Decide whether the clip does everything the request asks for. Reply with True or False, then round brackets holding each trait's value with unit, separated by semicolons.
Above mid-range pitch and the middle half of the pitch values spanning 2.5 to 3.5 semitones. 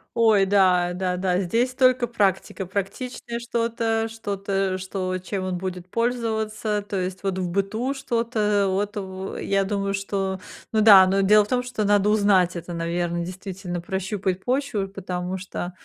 True (195 Hz; 2.8 semitones)